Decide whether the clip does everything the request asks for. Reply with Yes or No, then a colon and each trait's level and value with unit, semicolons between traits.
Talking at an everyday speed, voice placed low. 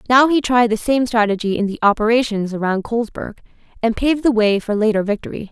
No: average, 185 wpm; high, 225 Hz